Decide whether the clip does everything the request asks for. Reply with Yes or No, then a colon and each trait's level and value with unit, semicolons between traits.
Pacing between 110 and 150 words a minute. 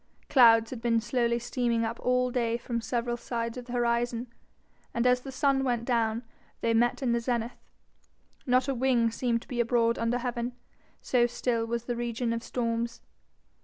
No: average, 180 wpm